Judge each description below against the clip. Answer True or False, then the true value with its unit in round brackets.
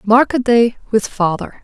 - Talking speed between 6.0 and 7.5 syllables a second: False (4.3 syllables/s)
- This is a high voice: True (225 Hz)